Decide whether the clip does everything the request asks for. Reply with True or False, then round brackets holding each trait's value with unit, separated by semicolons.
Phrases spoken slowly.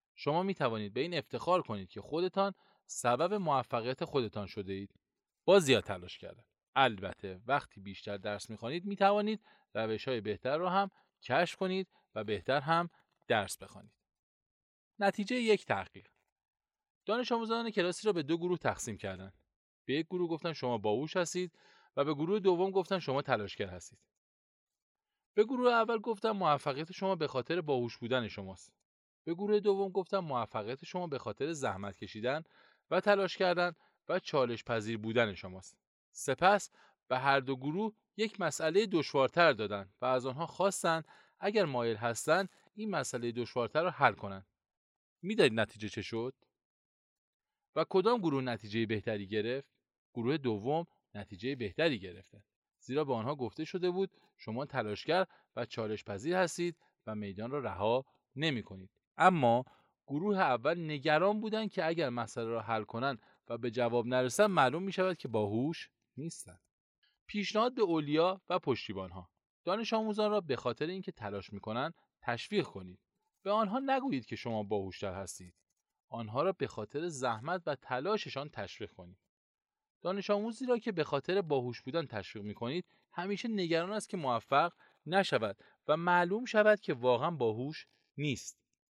False (155 wpm)